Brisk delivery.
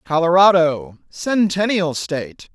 No: slow, 70 wpm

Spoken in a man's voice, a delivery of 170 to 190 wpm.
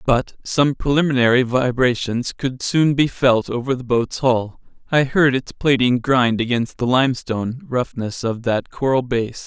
No: male; average, 160 wpm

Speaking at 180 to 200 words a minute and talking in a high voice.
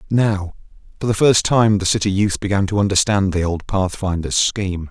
No: average, 185 wpm; low, 100 Hz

